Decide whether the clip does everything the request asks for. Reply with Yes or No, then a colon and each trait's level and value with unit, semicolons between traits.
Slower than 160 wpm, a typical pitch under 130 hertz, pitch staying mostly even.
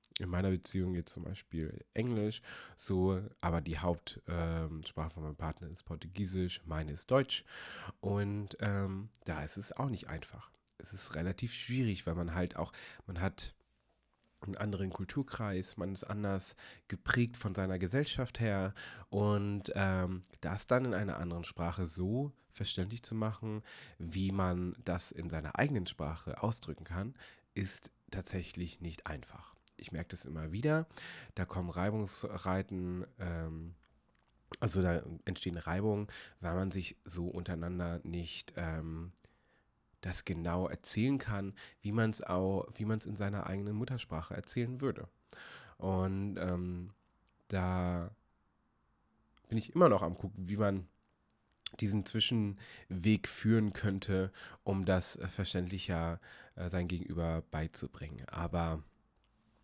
No: average, 130 wpm; very low, 95 Hz; average, 3.4 semitones